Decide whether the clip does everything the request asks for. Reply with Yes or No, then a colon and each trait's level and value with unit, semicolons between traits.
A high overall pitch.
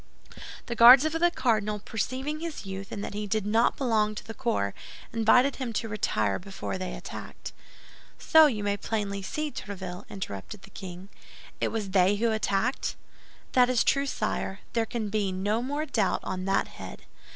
Yes: high, 215 Hz